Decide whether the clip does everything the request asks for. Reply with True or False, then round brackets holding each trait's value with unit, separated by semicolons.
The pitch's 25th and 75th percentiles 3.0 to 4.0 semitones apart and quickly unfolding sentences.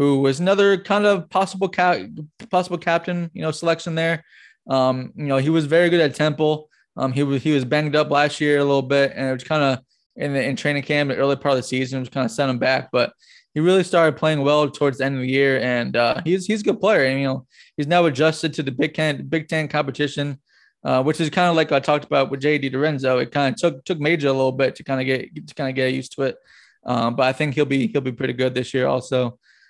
True (3.4 semitones; 270 wpm)